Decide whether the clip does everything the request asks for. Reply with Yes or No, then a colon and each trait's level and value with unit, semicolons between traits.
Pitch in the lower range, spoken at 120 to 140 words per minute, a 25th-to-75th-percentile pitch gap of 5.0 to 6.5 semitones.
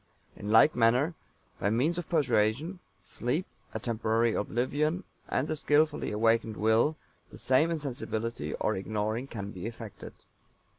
Yes: low, 120 Hz; slow, 135 wpm; wide, 5.4 semitones